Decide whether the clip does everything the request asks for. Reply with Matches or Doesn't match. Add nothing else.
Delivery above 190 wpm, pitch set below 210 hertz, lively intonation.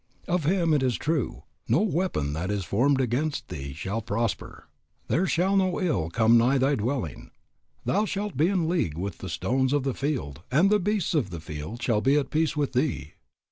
Matches